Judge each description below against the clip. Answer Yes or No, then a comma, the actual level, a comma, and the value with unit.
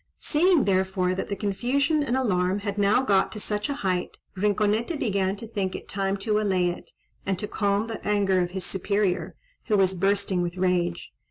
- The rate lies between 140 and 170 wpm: No, average, 190 wpm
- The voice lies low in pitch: No, high, 200 Hz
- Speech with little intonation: Yes, narrow, 2.3 semitones